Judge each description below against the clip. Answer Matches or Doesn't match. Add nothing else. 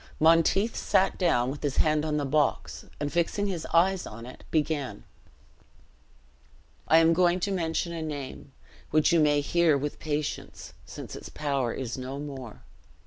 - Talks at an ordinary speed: Matches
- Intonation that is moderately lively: Matches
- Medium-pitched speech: Matches